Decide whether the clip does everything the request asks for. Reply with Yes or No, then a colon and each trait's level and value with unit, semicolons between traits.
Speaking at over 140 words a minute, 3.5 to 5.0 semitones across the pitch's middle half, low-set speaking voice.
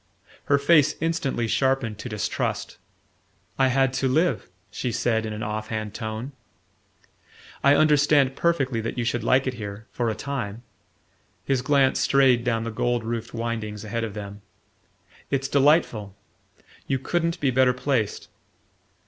Yes: average, 150 wpm; average, 3.8 semitones; low, 125 Hz